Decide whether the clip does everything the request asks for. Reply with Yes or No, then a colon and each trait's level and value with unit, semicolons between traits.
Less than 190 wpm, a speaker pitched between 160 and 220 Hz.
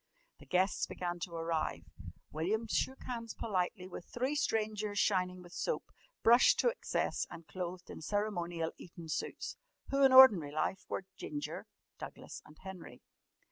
Yes: average, 145 wpm; medium, 185 Hz